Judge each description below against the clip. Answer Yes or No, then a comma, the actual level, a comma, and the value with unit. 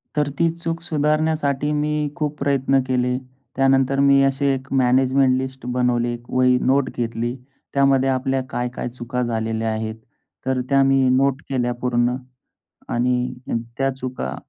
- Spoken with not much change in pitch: Yes, narrow, 2.0 semitones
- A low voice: Yes, low, 130 Hz